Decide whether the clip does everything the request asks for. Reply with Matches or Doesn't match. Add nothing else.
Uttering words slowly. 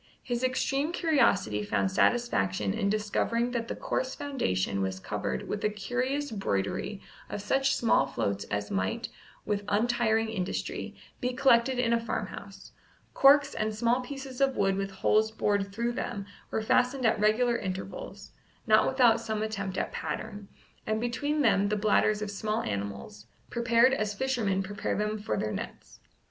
Doesn't match